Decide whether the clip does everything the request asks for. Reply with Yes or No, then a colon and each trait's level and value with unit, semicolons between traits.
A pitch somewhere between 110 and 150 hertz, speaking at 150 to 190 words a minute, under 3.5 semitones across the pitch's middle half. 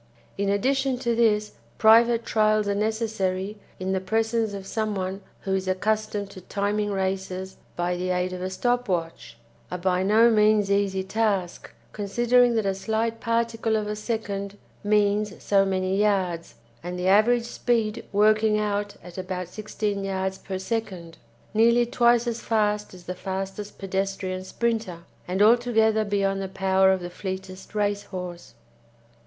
No: high, 205 Hz; average, 155 wpm; narrow, 2.5 semitones